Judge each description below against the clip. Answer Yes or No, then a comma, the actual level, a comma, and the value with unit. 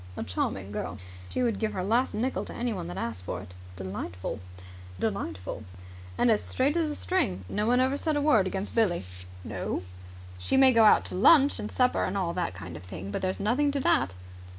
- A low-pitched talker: No, high, 210 Hz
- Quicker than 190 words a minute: Yes, fast, 205 wpm